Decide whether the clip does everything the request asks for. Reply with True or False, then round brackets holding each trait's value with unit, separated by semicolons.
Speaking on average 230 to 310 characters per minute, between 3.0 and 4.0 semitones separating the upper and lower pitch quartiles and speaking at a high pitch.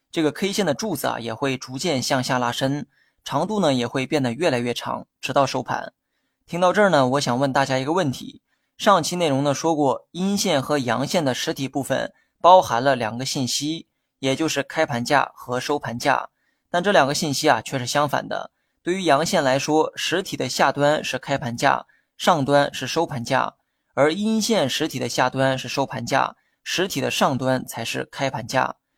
False (275 characters per minute; 3.6 semitones; 140 Hz)